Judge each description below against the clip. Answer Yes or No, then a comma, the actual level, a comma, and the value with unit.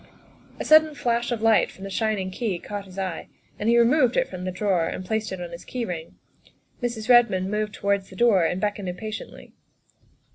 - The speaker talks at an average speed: No, fast, 210 wpm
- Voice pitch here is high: Yes, high, 205 Hz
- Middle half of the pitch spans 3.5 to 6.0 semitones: Yes, average, 3.9 semitones